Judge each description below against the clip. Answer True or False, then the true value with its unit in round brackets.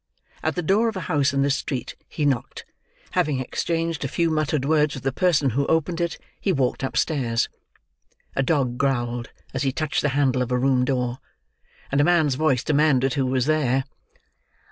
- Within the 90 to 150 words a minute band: False (190 wpm)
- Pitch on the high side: False (140 Hz)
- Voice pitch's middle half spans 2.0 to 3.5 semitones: True (3.1 semitones)